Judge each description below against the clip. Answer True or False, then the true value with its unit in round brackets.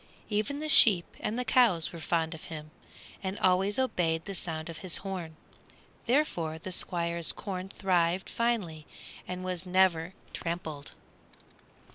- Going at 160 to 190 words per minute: False (140 wpm)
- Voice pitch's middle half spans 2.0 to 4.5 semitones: True (3.2 semitones)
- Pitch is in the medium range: True (180 Hz)